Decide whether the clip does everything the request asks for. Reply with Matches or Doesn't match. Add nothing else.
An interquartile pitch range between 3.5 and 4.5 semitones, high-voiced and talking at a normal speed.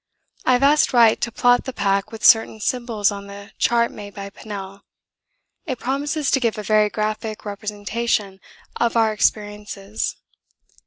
Doesn't match